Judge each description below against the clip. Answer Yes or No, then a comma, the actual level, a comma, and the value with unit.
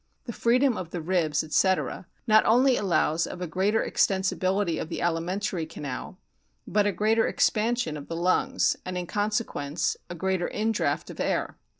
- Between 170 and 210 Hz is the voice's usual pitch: Yes, high, 190 Hz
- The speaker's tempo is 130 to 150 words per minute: No, average, 165 wpm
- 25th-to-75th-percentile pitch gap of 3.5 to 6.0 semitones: Yes, average, 4.2 semitones